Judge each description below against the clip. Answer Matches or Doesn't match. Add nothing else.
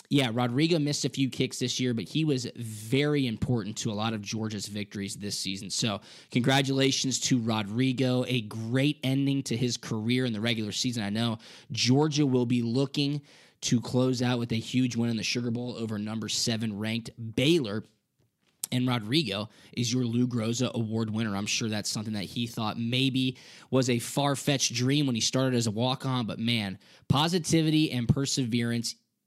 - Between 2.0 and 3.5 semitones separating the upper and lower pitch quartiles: Matches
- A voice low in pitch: Matches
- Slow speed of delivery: Doesn't match